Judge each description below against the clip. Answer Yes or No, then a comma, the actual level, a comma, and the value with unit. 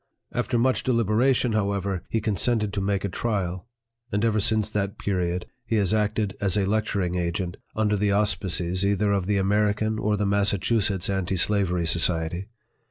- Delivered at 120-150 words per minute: No, average, 165 wpm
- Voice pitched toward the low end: Yes, low, 100 Hz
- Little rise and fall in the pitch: Yes, narrow, 2.3 semitones